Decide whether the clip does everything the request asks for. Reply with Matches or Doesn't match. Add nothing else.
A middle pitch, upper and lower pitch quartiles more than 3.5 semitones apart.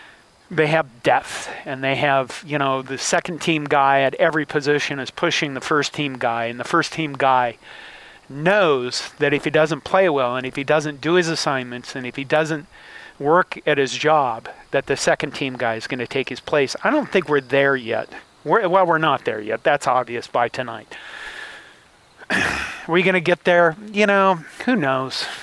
Matches